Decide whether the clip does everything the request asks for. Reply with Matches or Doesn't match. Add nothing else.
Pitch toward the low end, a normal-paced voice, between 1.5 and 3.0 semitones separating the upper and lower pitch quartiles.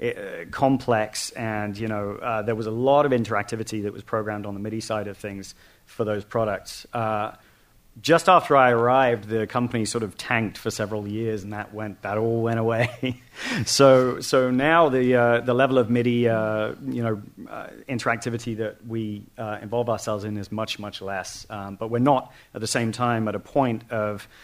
Matches